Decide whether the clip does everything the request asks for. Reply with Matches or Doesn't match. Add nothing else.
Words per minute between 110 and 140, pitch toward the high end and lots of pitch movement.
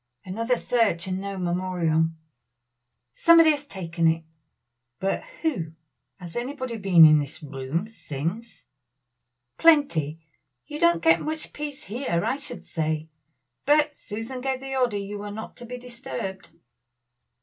Matches